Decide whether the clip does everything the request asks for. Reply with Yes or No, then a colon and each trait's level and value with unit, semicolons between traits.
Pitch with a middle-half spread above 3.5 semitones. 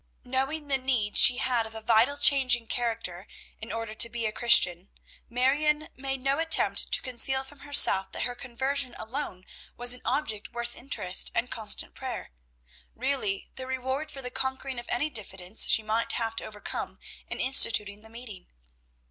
No: average, 3.2 semitones